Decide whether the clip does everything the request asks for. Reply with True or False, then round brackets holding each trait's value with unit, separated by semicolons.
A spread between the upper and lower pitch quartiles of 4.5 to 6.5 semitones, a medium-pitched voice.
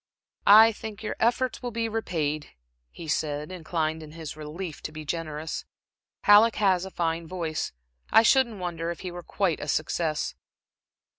True (5.0 semitones; 170 Hz)